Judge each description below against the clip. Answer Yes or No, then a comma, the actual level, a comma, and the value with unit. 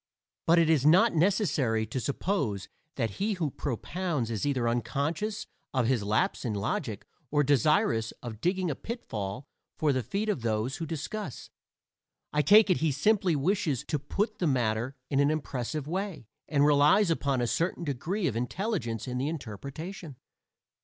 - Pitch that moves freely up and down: Yes, wide, 6.6 semitones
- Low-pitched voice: No, medium, 145 Hz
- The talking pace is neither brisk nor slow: Yes, average, 165 wpm